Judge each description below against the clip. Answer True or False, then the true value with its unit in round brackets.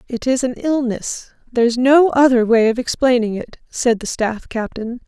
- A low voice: False (245 Hz)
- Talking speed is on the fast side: False (175 wpm)